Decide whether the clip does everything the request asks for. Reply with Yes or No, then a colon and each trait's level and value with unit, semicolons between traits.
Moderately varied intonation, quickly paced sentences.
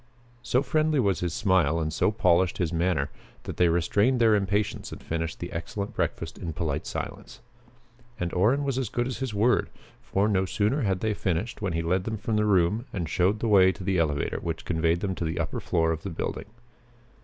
Yes: average, 4.4 semitones; fast, 210 wpm